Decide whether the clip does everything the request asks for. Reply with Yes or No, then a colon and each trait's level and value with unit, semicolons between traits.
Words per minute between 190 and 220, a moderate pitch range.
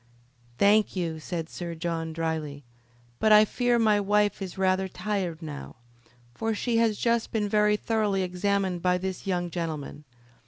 No: average, 155 wpm; average, 3.9 semitones